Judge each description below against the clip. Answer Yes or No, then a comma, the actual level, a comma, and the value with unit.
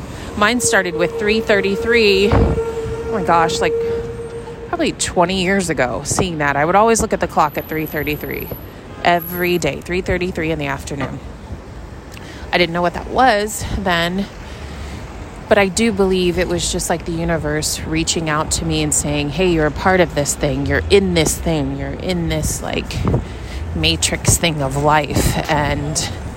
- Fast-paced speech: No, average, 165 wpm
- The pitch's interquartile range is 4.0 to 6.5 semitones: Yes, average, 4.5 semitones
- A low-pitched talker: No, medium, 175 Hz